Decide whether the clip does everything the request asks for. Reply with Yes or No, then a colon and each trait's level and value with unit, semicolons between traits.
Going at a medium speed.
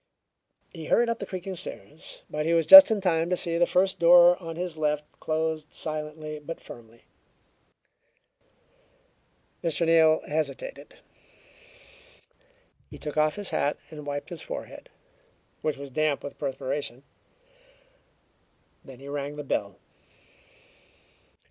No: slow, 130 wpm